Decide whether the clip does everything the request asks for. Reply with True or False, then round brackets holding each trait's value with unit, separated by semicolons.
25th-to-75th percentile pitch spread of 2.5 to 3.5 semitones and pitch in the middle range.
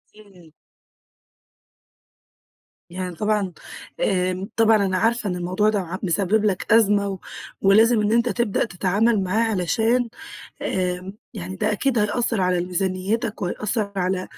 False (3.2 semitones; 200 Hz)